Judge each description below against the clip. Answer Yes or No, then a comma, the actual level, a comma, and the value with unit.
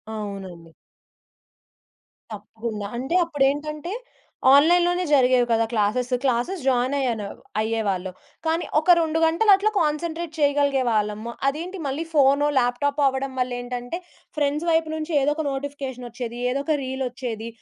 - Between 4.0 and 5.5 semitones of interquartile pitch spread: Yes, average, 4.5 semitones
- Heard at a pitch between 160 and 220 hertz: No, very high, 270 Hz